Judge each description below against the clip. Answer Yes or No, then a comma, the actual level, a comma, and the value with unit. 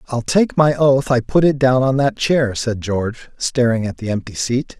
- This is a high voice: No, low, 125 Hz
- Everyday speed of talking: No, fast, 225 wpm